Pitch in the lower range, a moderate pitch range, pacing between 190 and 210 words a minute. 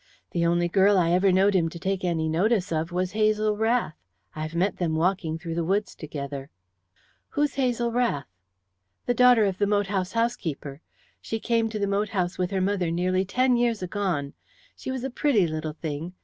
No: high, 190 Hz; average, 4.3 semitones; average, 200 wpm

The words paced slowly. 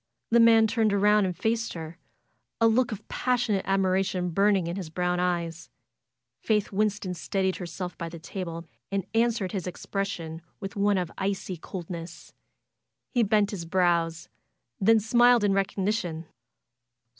No: average, 145 wpm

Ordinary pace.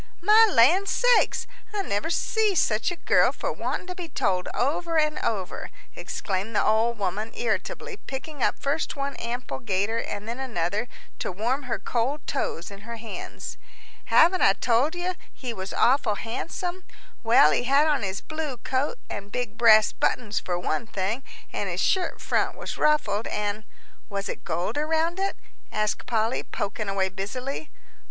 Yes: average, 170 wpm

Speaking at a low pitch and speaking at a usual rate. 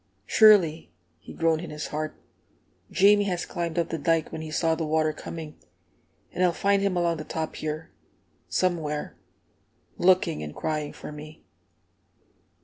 No: medium, 160 Hz; average, 150 wpm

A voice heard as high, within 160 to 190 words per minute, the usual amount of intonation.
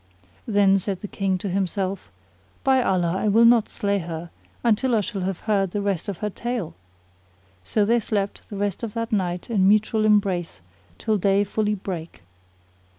No: high, 200 Hz; average, 175 wpm; narrow, 2.3 semitones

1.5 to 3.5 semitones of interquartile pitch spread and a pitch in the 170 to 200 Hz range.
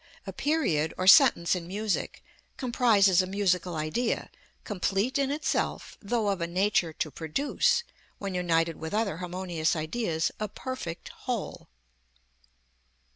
No: average, 5.2 semitones; high, 190 Hz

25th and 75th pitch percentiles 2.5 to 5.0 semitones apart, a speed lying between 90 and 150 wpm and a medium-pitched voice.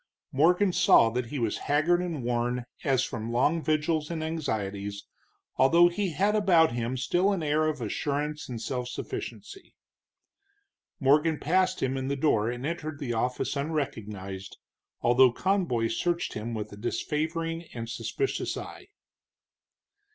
No: wide, 5.6 semitones; average, 145 wpm; medium, 145 Hz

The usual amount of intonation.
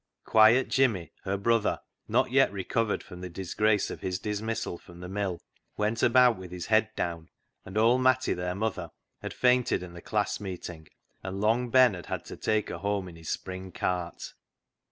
Yes: average, 3.8 semitones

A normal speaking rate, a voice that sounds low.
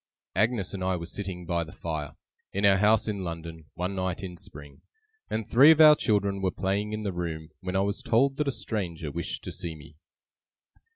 No: fast, 210 wpm; very low, 95 Hz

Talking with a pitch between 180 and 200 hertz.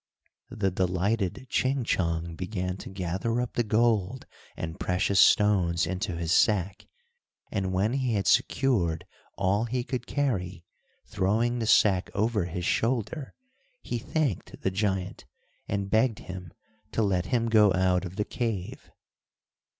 No: low, 100 Hz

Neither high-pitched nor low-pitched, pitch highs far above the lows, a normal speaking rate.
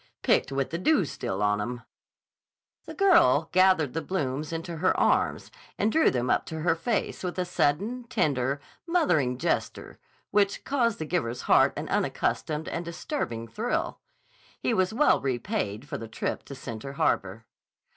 Yes: medium, 160 Hz; wide, 8.0 semitones; average, 160 wpm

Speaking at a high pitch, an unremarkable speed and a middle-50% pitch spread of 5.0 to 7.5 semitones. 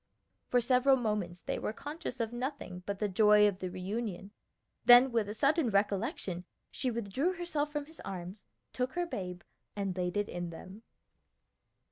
Yes: high, 210 Hz; average, 165 wpm; wide, 5.5 semitones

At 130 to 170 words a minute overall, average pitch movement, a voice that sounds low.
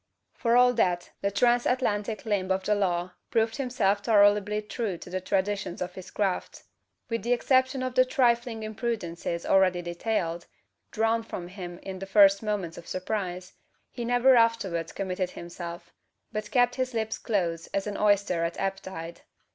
No: average, 165 wpm; average, 4.0 semitones; high, 205 Hz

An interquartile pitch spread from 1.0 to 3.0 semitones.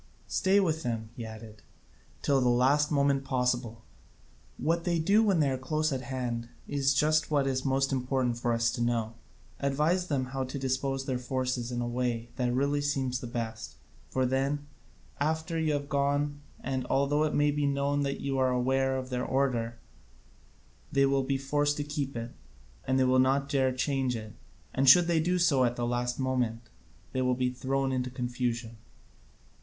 Yes: narrow, 2.4 semitones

